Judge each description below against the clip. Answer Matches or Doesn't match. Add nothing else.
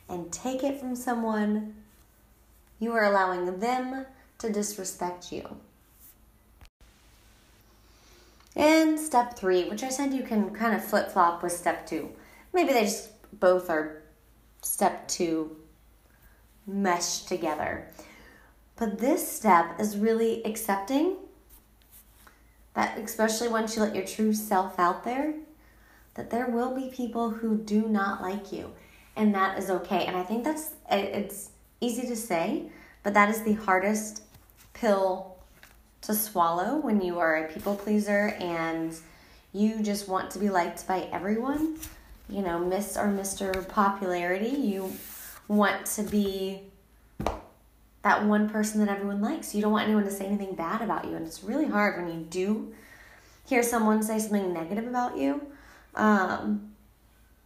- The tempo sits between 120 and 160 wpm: Matches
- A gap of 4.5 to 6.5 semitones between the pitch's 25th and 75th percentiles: Doesn't match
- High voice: Matches